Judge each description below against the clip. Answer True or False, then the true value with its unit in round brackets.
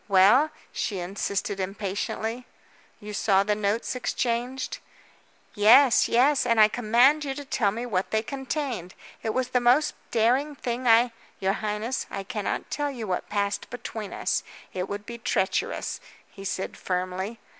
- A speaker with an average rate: True (155 wpm)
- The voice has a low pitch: False (225 Hz)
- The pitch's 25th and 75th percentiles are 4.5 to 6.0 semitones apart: False (3.9 semitones)